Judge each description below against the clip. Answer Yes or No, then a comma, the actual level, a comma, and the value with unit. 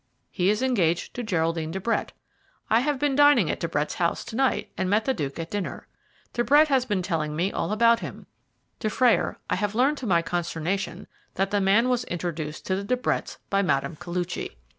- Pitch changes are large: Yes, wide, 6.0 semitones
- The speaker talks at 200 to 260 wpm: Yes, fast, 205 wpm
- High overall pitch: Yes, high, 200 Hz